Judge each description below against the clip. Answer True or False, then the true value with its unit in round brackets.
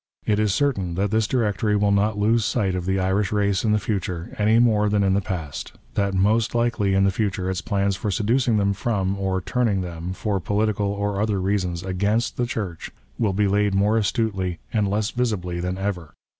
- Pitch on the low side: True (100 Hz)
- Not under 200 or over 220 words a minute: True (205 wpm)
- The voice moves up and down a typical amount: False (2.2 semitones)